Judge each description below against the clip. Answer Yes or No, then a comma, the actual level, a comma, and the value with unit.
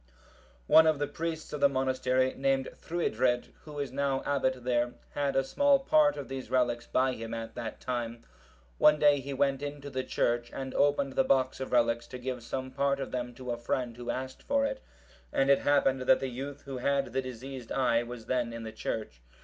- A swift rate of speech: Yes, fast, 210 wpm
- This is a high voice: No, low, 130 Hz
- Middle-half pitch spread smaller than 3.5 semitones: Yes, narrow, 2.4 semitones